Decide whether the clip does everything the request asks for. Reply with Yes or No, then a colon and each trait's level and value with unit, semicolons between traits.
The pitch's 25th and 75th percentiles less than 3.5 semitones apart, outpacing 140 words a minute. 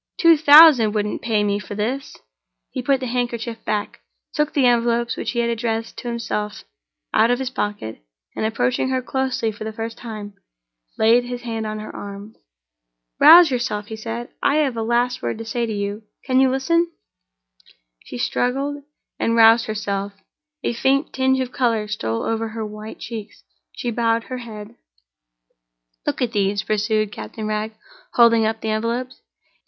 Yes: average, 2.8 semitones; average, 165 wpm